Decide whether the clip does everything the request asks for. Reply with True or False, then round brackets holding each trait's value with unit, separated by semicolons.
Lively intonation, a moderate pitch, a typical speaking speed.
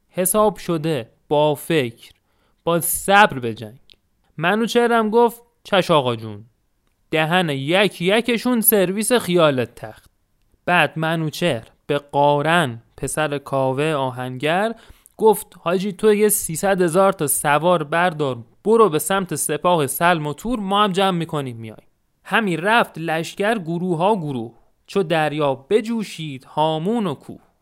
True (6.1 semitones; 165 Hz; 125 wpm)